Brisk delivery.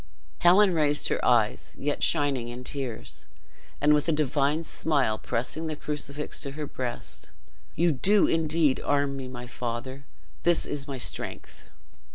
No: average, 155 wpm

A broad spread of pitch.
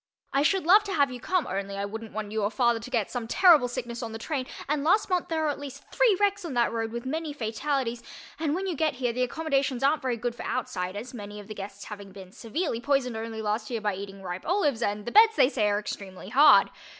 Yes: wide, 5.7 semitones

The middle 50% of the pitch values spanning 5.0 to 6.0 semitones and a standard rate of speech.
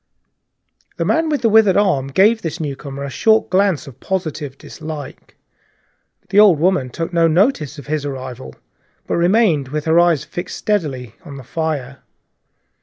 Yes: wide, 5.4 semitones; average, 160 wpm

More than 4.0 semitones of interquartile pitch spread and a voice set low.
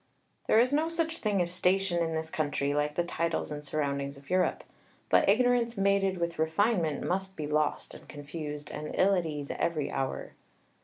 No: average, 4.7 semitones; medium, 170 Hz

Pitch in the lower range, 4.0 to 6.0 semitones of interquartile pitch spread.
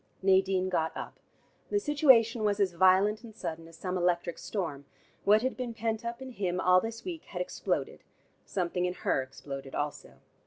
No: high, 190 Hz; average, 4.6 semitones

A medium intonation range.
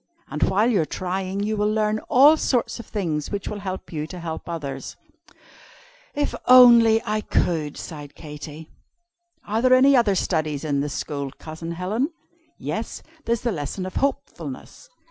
No: wide, 6.5 semitones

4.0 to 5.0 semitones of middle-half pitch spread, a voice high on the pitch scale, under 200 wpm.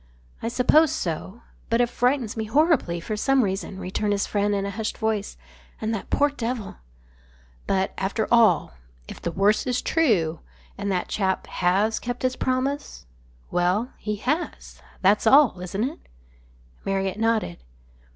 Yes: average, 4.4 semitones; high, 215 Hz; average, 160 wpm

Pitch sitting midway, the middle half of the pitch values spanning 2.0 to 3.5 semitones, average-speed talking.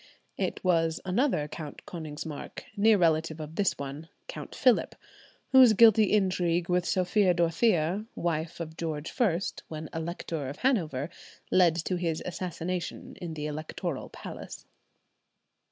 No: medium, 170 Hz; average, 2.9 semitones; slow, 130 wpm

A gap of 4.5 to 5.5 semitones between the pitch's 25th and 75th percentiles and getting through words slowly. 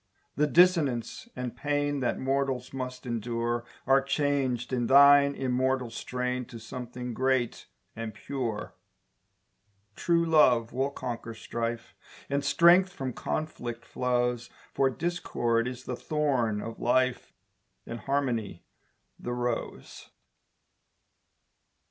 No: average, 2.9 semitones; slow, 110 wpm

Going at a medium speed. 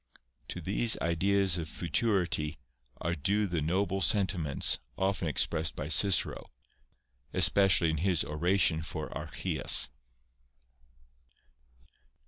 No: slow, 105 wpm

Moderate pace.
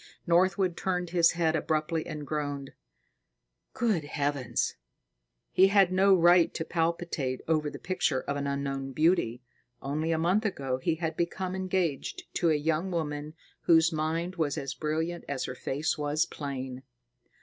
Yes: average, 150 wpm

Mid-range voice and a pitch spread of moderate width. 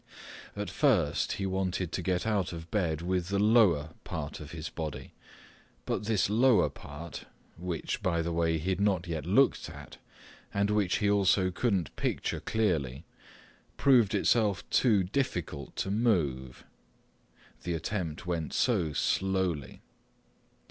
No: very low, 90 Hz; average, 4.0 semitones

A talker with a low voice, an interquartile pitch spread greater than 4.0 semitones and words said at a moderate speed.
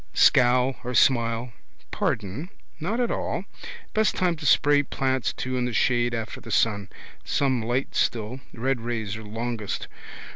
No: low, 120 Hz; average, 2.8 semitones; average, 150 wpm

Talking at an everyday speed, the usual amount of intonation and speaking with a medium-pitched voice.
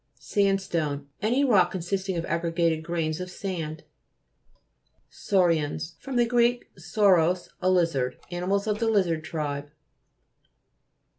No: slow, 105 wpm; average, 3.6 semitones; medium, 175 Hz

